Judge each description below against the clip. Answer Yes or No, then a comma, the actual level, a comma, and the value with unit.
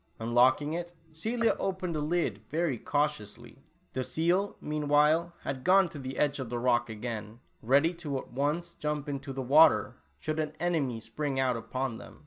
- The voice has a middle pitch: Yes, medium, 145 Hz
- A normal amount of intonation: Yes, average, 4.5 semitones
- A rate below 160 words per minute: No, average, 170 wpm